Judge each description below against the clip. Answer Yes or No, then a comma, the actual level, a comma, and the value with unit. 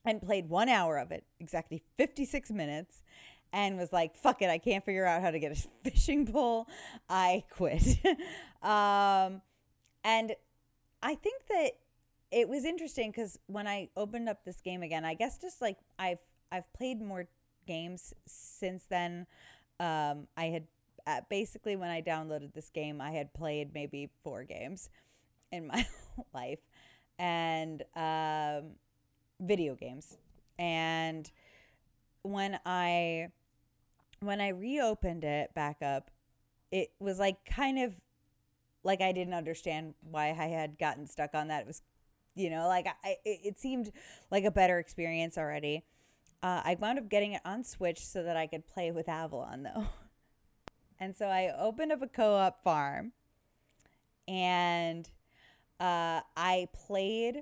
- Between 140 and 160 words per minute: Yes, average, 150 wpm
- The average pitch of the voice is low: No, medium, 180 Hz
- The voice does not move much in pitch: No, average, 4.7 semitones